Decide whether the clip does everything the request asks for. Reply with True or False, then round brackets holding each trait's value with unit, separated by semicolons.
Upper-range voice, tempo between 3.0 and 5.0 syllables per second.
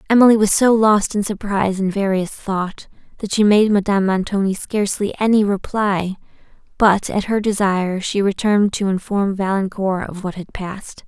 False (200 Hz; 5.2 syllables/s)